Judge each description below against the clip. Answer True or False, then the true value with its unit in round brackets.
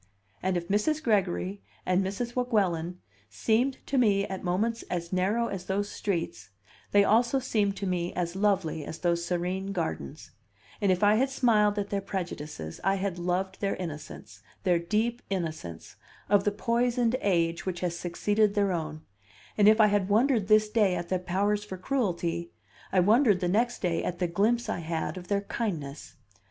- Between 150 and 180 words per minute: True (175 wpm)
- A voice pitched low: False (195 Hz)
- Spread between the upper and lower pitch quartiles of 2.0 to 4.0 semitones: True (3.5 semitones)